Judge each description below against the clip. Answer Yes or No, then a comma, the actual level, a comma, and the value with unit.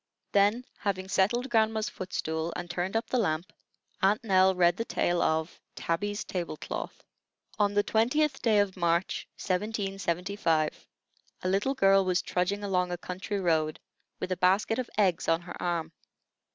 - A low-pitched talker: No, high, 190 Hz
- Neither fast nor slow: Yes, average, 160 wpm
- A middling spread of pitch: Yes, average, 3.0 semitones